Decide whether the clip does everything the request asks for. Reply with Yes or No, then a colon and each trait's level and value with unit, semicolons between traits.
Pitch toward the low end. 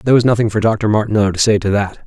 Yes: low, 110 Hz